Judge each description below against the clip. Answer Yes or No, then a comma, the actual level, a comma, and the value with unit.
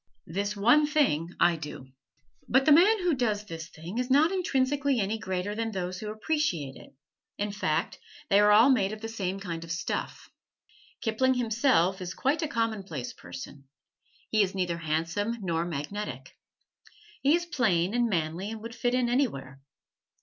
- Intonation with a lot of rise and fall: Yes, wide, 6.5 semitones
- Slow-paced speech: No, average, 170 wpm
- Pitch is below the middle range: No, high, 210 Hz